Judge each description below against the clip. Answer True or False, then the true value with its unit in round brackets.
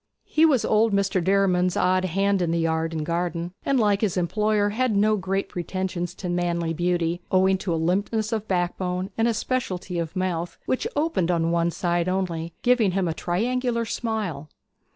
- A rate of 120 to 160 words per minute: False (175 wpm)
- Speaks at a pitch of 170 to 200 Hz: True (185 Hz)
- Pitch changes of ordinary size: True (3.5 semitones)